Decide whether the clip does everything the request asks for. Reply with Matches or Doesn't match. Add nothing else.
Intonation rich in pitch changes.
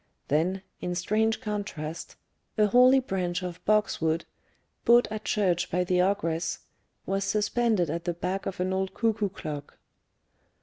Doesn't match